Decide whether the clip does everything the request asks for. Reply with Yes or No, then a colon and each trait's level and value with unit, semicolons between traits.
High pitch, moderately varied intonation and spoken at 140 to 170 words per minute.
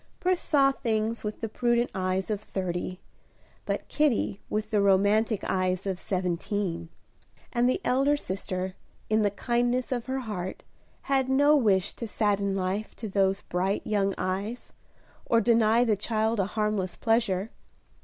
Yes: high, 210 Hz; average, 3.8 semitones; average, 150 wpm